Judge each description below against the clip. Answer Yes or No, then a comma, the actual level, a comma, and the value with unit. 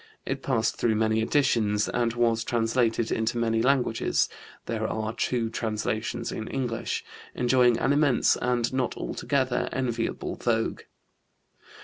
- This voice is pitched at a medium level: No, low, 115 Hz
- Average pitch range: No, narrow, 1.8 semitones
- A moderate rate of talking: No, slow, 125 wpm